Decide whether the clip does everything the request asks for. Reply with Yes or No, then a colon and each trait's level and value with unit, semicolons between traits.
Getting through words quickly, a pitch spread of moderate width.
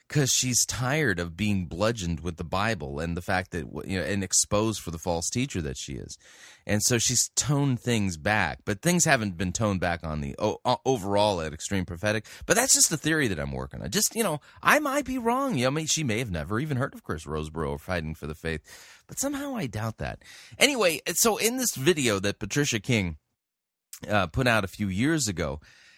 No: fast, 220 wpm; wide, 7.3 semitones